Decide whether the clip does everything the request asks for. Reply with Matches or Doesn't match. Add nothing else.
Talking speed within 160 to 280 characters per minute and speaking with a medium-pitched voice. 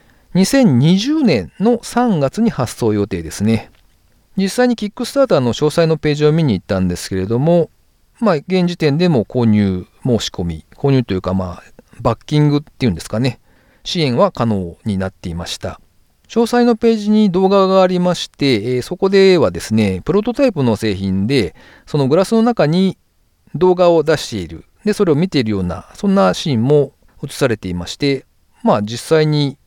Doesn't match